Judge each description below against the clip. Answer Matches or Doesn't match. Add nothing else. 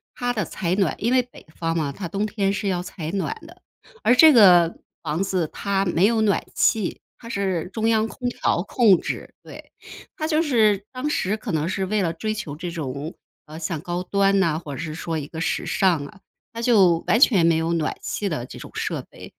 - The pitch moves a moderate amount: Matches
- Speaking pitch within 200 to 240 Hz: Doesn't match